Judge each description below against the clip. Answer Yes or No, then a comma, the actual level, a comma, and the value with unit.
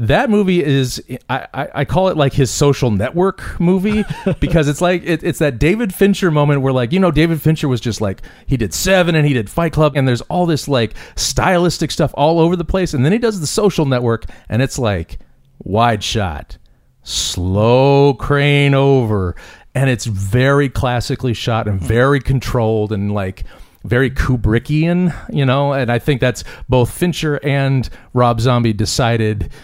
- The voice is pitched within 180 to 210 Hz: No, low, 135 Hz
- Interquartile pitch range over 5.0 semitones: Yes, wide, 5.4 semitones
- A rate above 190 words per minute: No, average, 180 wpm